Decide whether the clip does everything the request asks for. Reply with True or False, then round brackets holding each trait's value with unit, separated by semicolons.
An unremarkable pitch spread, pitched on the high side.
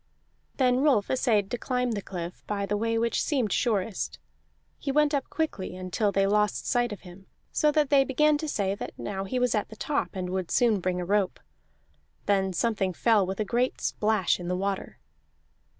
True (4.5 semitones; 210 Hz)